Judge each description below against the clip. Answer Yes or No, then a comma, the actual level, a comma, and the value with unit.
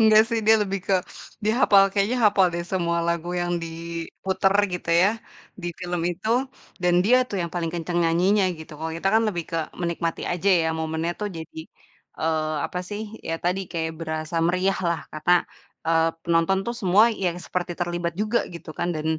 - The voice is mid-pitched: Yes, medium, 175 Hz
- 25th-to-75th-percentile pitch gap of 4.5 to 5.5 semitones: No, average, 2.7 semitones